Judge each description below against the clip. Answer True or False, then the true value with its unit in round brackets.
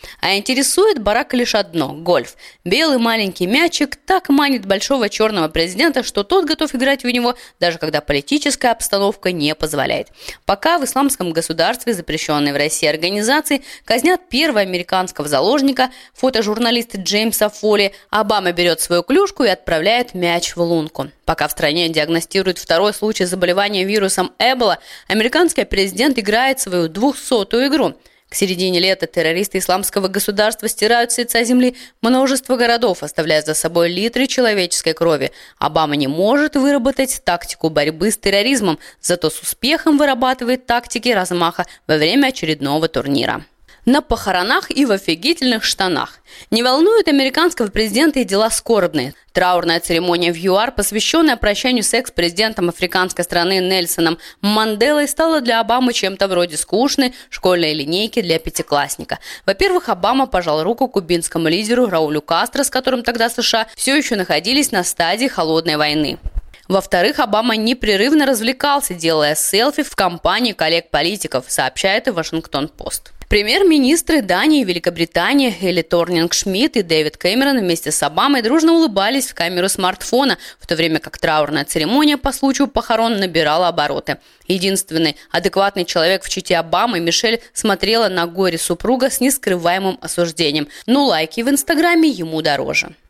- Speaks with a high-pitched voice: True (205 Hz)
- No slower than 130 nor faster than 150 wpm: True (140 wpm)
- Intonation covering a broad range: True (7.2 semitones)